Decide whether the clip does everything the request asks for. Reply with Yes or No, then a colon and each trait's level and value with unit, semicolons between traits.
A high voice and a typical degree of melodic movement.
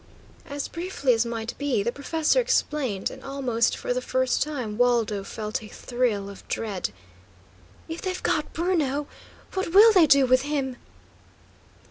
Yes: very high, 260 Hz; average, 4.8 semitones